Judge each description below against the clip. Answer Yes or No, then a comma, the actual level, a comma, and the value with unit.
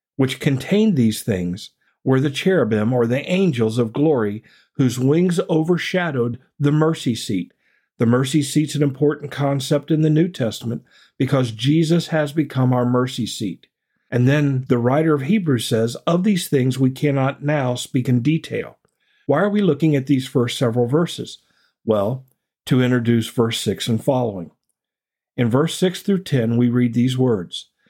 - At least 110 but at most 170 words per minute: Yes, average, 165 wpm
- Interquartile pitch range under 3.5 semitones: No, average, 4.2 semitones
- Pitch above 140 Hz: No, low, 135 Hz